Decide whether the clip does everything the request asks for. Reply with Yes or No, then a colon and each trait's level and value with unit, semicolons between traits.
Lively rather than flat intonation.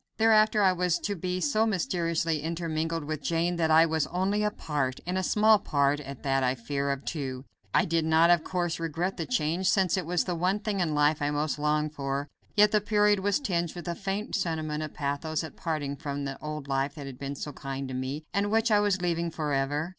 No: average, 4.2 semitones